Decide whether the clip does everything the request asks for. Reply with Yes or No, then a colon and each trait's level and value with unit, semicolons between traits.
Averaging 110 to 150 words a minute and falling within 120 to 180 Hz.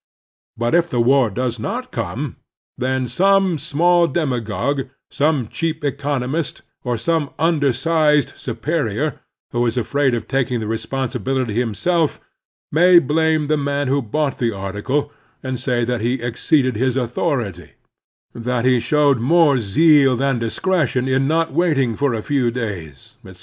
Yes: average, 145 wpm; low, 135 Hz